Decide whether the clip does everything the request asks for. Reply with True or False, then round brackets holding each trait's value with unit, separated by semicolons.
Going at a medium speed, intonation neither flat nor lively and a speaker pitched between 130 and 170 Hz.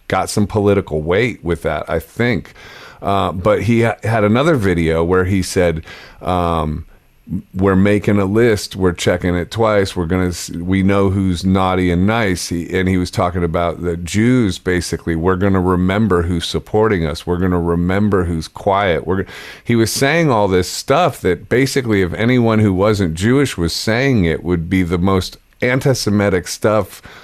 False (185 wpm; 3.2 semitones; 95 Hz)